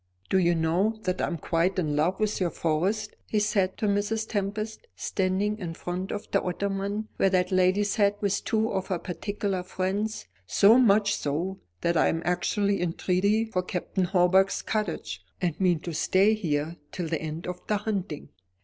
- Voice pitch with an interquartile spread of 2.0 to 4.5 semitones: Yes, average, 2.7 semitones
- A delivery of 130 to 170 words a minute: No, average, 185 wpm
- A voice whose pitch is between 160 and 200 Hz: Yes, high, 190 Hz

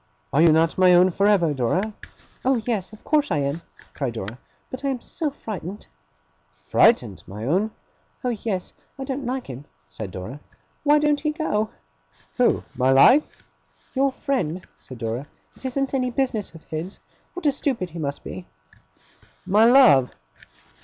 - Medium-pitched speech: No, high, 195 Hz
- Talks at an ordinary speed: Yes, average, 165 wpm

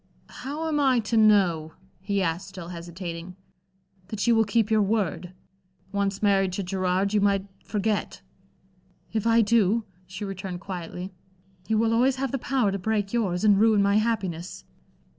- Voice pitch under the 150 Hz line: No, high, 200 Hz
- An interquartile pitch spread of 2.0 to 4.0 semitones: Yes, average, 3.2 semitones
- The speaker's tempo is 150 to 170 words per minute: Yes, average, 160 wpm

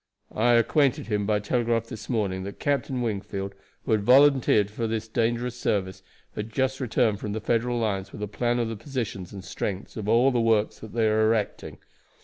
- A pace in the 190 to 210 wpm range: Yes, average, 195 wpm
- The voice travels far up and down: No, narrow, 2.6 semitones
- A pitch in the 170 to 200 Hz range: No, low, 110 Hz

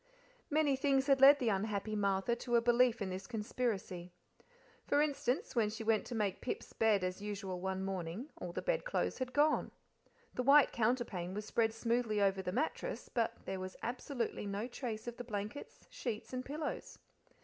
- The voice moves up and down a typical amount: Yes, average, 4.2 semitones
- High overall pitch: Yes, high, 225 Hz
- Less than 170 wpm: No, average, 180 wpm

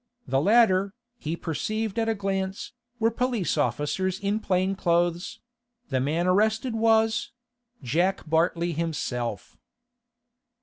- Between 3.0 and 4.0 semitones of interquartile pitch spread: No, average, 4.8 semitones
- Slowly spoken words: Yes, slow, 105 wpm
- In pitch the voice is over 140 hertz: Yes, high, 190 Hz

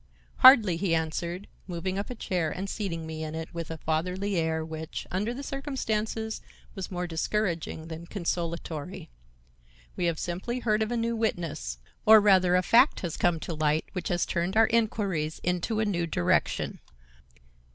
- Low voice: No, medium, 180 Hz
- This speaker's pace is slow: No, average, 170 wpm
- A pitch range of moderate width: Yes, average, 4.6 semitones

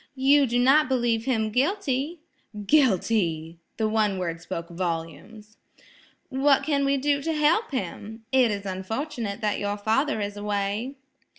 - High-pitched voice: Yes, high, 225 Hz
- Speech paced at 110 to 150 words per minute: Yes, average, 140 wpm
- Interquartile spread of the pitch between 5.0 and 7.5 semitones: Yes, wide, 5.4 semitones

